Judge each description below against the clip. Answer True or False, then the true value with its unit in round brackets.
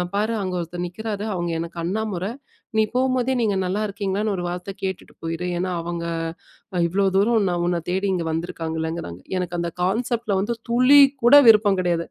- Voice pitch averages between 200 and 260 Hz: False (190 Hz)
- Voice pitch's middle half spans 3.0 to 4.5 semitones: True (3.9 semitones)